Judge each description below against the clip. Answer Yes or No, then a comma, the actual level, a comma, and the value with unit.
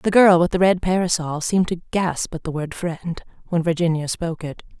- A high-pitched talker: No, medium, 170 Hz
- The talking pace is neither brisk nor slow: No, fast, 215 wpm